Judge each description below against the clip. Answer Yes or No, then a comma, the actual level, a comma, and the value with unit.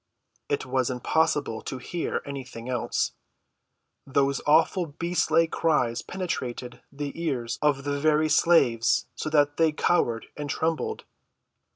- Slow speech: Yes, slow, 120 wpm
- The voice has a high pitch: No, medium, 145 Hz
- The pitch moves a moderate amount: Yes, average, 3.9 semitones